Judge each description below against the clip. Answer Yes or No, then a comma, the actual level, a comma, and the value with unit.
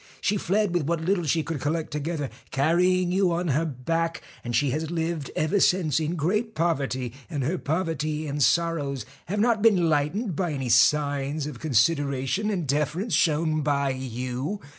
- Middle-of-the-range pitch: Yes, medium, 155 Hz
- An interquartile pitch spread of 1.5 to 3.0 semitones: No, average, 3.7 semitones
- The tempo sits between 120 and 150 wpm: No, average, 170 wpm